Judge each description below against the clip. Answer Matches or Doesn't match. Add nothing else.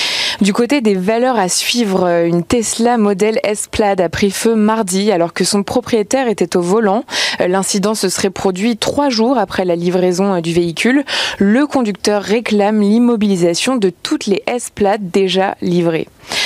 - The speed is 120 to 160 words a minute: Matches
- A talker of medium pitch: Doesn't match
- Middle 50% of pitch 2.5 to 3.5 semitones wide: Doesn't match